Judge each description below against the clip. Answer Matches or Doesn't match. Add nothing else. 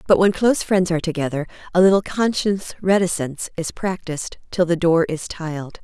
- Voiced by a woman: Matches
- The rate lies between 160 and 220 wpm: Matches